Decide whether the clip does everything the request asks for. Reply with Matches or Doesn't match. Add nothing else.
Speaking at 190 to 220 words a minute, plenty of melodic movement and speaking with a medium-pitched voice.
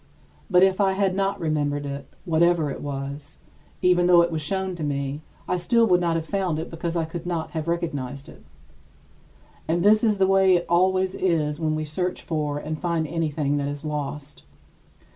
Doesn't match